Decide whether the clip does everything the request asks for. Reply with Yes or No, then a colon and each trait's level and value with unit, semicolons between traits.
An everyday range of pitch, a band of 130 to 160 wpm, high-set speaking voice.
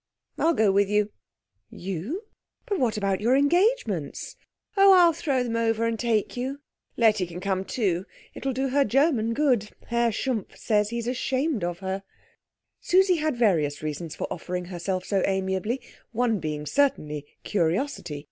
No: wide, 6.1 semitones; average, 155 wpm; high, 225 Hz